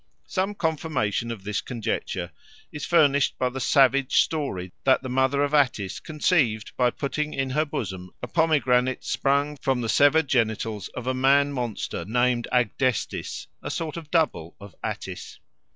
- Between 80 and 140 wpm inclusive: No, average, 155 wpm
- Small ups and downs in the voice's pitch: No, average, 4.0 semitones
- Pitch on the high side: No, low, 130 Hz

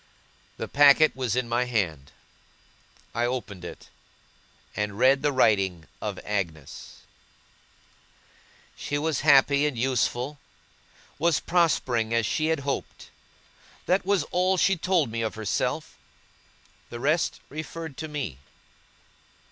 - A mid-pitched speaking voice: No, low, 130 Hz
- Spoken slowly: Yes, slow, 120 wpm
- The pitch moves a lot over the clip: Yes, wide, 5.9 semitones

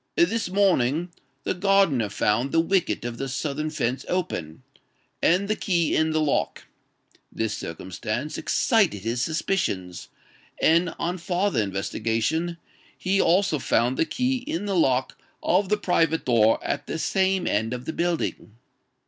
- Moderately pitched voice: Yes, medium, 160 Hz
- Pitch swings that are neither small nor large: No, wide, 7.3 semitones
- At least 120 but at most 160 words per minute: Yes, average, 145 wpm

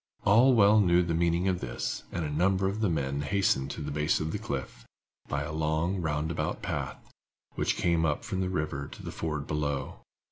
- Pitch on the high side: No, very low, 80 Hz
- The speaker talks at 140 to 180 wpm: No, fast, 205 wpm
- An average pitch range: Yes, average, 4.1 semitones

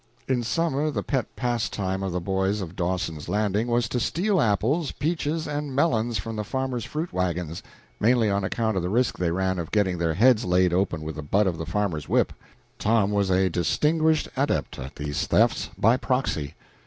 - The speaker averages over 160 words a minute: Yes, average, 190 wpm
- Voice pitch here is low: Yes, low, 105 Hz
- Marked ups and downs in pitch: Yes, wide, 6.0 semitones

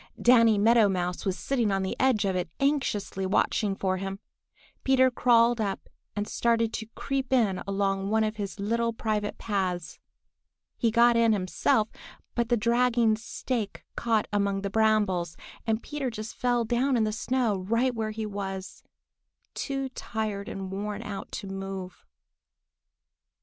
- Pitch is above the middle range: Yes, high, 215 Hz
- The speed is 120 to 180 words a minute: Yes, average, 155 wpm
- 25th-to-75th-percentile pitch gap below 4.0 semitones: Yes, average, 3.2 semitones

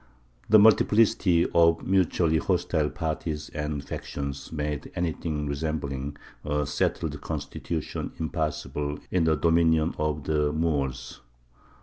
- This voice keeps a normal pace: No, slow, 105 wpm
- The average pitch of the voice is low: Yes, very low, 75 Hz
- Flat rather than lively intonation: Yes, narrow, 2.1 semitones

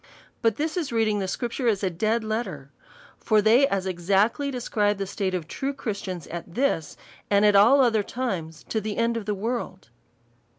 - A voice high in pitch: Yes, high, 215 Hz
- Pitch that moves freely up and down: No, average, 3.7 semitones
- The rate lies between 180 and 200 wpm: Yes, average, 185 wpm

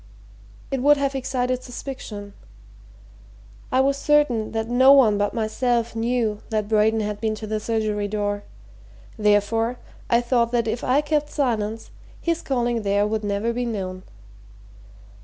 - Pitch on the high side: Yes, high, 225 Hz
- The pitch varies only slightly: No, average, 3.1 semitones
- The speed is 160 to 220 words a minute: No, average, 145 wpm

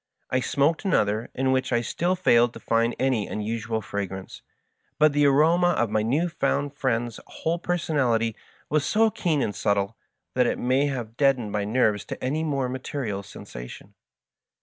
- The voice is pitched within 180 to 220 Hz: No, low, 130 Hz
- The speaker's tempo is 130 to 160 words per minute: No, average, 170 wpm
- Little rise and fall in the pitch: No, average, 4.7 semitones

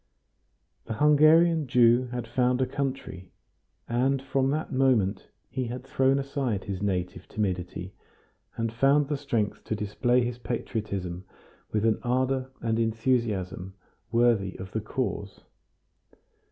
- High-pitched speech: No, low, 120 Hz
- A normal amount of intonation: Yes, average, 4.5 semitones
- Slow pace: Yes, slow, 125 wpm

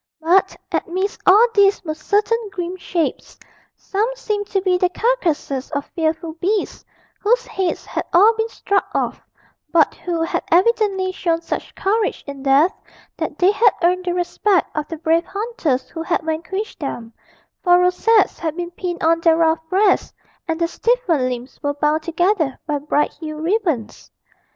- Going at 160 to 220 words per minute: Yes, average, 165 wpm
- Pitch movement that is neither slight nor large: Yes, average, 3.9 semitones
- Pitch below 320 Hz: No, very high, 350 Hz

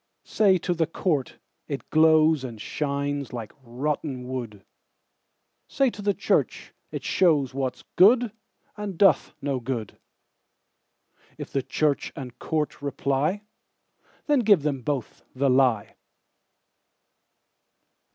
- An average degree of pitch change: Yes, average, 4.6 semitones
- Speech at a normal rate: No, slow, 95 wpm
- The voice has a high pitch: No, medium, 140 Hz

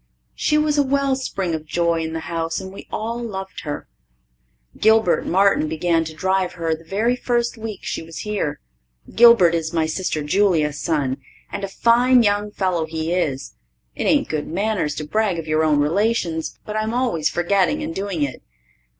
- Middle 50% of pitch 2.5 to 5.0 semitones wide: No, wide, 5.4 semitones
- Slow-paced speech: No, average, 185 wpm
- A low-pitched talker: No, medium, 185 Hz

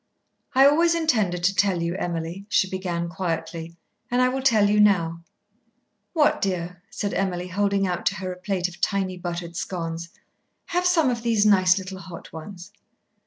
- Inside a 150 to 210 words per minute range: Yes, average, 170 wpm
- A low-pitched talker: No, medium, 185 Hz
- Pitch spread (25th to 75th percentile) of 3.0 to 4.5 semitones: Yes, average, 3.3 semitones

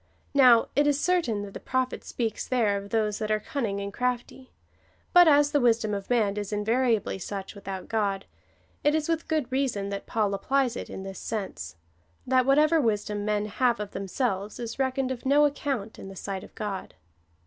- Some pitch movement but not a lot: Yes, average, 4.6 semitones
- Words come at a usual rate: Yes, average, 195 wpm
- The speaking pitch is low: No, high, 225 Hz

